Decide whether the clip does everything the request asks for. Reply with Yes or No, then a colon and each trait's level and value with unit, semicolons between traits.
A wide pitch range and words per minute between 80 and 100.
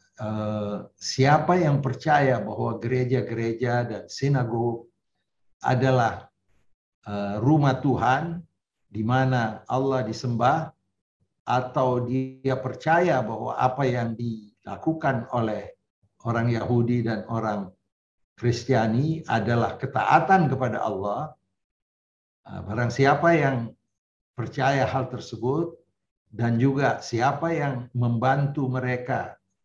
No: average, 3.1 semitones; slow, 85 wpm